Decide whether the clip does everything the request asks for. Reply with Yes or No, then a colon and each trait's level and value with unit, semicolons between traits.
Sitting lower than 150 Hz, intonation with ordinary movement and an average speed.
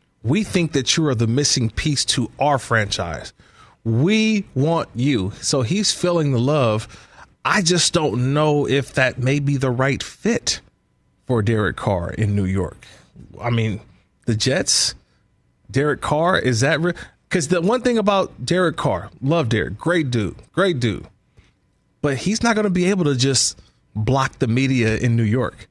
No: low, 135 Hz; wide, 6.4 semitones; average, 170 wpm